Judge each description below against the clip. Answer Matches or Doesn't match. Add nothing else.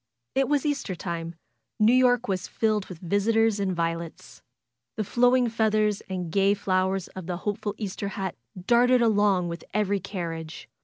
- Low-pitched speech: Doesn't match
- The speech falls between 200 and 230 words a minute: Doesn't match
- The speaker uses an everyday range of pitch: Matches